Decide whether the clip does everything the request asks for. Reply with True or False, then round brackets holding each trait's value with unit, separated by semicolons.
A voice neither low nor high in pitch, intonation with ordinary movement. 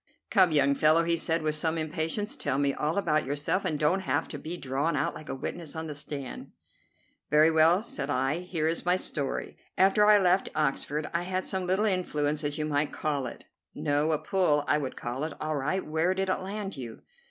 True (155 Hz; 3.8 semitones)